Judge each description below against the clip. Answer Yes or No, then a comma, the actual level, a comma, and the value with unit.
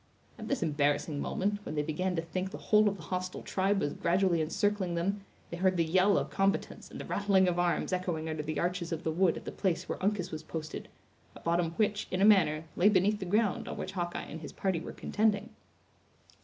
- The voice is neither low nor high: Yes, medium, 180 Hz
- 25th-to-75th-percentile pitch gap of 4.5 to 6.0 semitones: No, average, 3.2 semitones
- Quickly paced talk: Yes, fast, 225 wpm